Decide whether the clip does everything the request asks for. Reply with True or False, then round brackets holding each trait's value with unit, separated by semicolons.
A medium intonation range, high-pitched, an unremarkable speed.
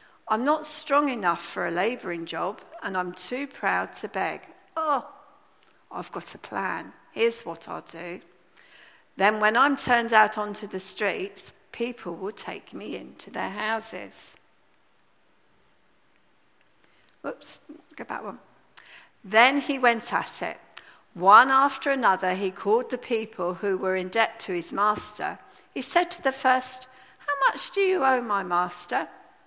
False (6.6 semitones; 240 Hz; 150 wpm)